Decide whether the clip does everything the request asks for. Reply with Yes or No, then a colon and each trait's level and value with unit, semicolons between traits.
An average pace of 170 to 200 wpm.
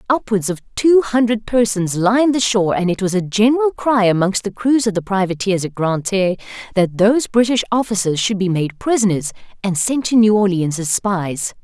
Yes: average, 195 wpm